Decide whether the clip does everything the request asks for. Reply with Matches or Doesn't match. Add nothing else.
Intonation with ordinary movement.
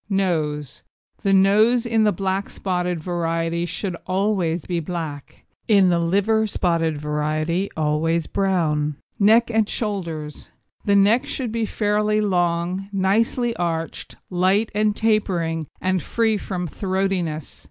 Matches